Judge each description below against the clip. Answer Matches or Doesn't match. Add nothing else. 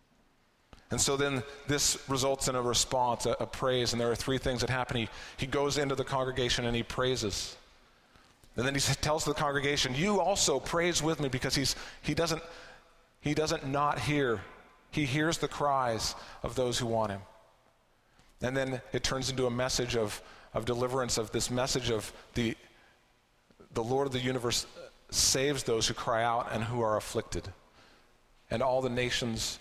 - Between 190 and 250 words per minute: Doesn't match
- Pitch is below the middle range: Matches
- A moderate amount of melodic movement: Matches